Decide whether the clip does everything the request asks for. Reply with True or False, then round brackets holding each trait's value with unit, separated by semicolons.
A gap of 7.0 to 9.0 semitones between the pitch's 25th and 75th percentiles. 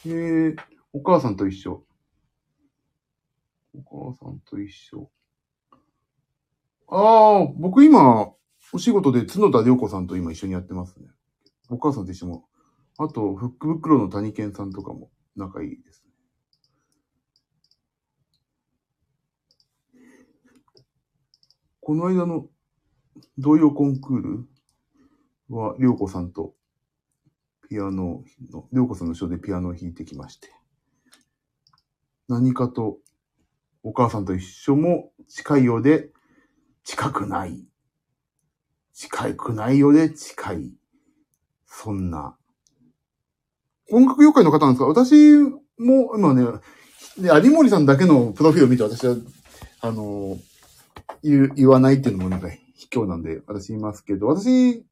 True (7.7 semitones)